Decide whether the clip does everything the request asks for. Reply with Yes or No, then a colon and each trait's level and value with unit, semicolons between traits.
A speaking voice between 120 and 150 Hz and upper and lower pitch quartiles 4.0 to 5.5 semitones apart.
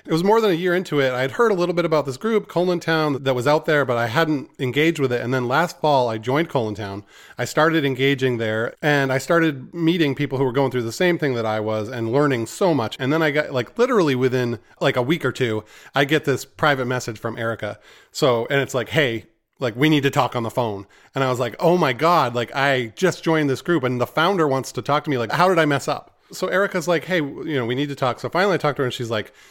Yes: medium, 140 Hz; average, 4.4 semitones